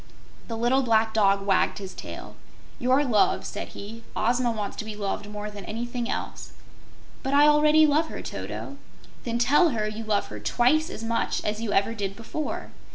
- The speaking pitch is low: No, high, 230 Hz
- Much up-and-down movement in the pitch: No, average, 3.9 semitones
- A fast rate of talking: No, average, 185 wpm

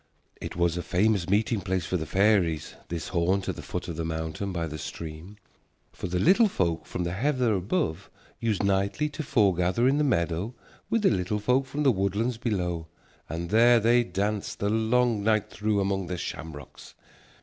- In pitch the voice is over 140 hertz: No, low, 100 Hz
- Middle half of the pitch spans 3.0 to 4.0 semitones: No, average, 4.9 semitones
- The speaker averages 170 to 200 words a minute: Yes, average, 185 wpm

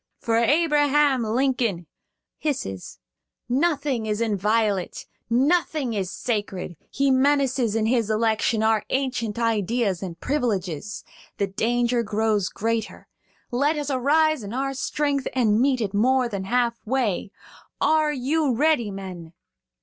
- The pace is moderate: No, slow, 120 wpm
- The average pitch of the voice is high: Yes, high, 235 Hz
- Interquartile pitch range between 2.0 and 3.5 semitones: No, average, 4.5 semitones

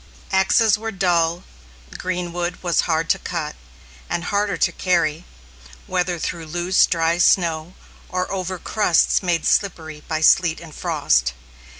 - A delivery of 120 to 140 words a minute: Yes, slow, 135 wpm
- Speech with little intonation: Yes, narrow, 2.1 semitones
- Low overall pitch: No, medium, 175 Hz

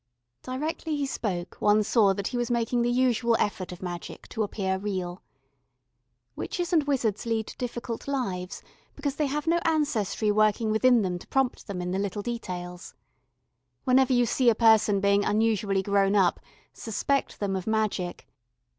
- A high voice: Yes, high, 220 Hz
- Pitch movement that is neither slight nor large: Yes, average, 4.3 semitones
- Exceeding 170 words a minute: No, average, 165 wpm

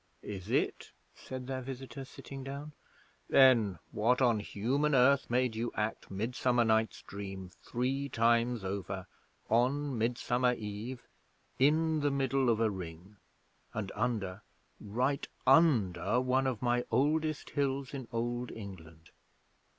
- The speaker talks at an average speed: No, slow, 125 wpm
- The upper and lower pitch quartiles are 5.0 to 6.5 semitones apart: No, average, 4.1 semitones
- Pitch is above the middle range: No, low, 120 Hz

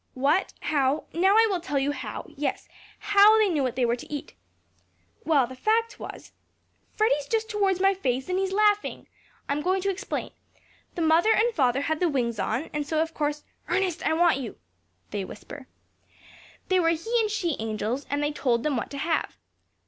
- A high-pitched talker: Yes, very high, 315 Hz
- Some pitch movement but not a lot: No, wide, 5.9 semitones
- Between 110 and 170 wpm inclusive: No, average, 195 wpm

